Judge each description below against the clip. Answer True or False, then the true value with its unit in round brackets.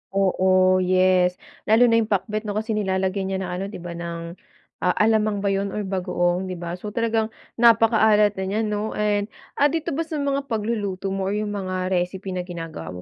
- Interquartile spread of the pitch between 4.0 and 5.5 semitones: False (2.8 semitones)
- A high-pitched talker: True (195 Hz)